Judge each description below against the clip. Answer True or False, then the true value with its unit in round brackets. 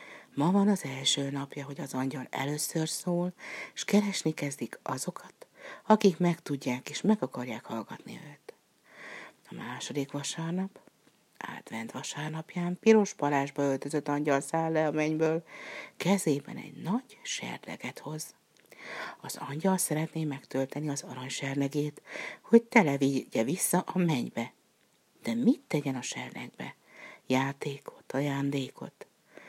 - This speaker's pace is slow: False (120 wpm)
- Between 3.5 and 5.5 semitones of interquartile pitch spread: True (4.1 semitones)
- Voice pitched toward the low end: False (150 Hz)